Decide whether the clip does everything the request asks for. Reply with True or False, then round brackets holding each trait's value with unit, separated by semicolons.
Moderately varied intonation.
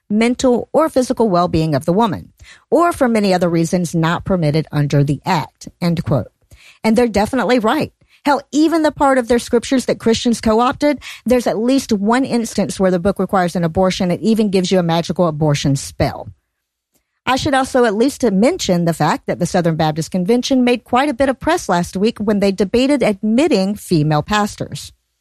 False (6.1 semitones)